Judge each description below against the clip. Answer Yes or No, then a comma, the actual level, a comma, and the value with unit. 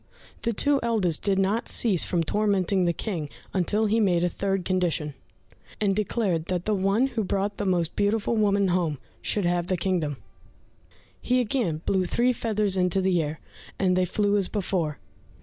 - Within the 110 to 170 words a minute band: No, average, 180 wpm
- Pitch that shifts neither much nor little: Yes, average, 3.0 semitones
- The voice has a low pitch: No, high, 195 Hz